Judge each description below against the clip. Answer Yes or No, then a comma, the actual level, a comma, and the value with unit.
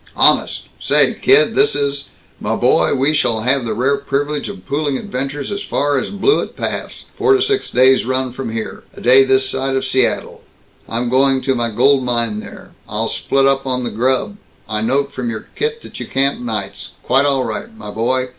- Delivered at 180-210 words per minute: Yes, average, 200 wpm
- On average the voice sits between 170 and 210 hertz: No, low, 135 Hz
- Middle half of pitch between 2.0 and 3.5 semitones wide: Yes, narrow, 2.5 semitones